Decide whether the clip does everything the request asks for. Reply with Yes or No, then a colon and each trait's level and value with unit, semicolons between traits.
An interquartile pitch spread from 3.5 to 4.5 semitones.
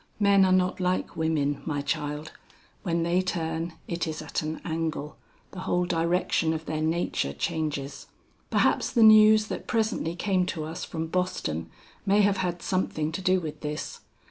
No: average, 2.9 semitones